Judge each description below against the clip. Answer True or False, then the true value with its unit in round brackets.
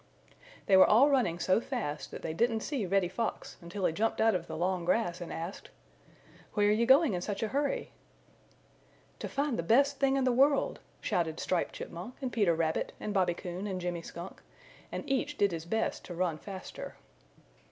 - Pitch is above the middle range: True (200 Hz)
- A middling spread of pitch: False (5.9 semitones)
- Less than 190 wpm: False (195 wpm)